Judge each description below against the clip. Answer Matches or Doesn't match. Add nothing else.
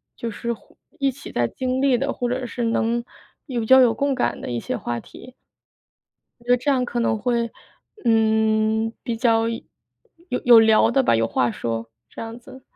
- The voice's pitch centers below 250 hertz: Matches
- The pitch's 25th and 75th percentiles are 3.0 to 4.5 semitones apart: Doesn't match